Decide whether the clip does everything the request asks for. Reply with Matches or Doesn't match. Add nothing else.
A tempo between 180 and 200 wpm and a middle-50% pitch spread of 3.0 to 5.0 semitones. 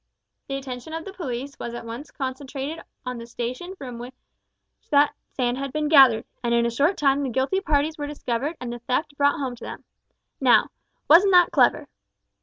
Matches